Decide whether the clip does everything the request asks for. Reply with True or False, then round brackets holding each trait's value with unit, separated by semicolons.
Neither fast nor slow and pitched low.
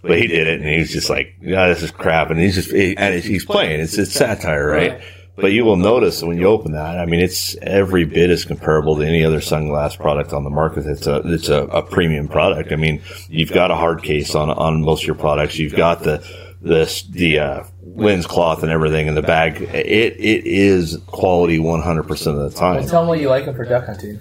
False (245 wpm; 85 Hz)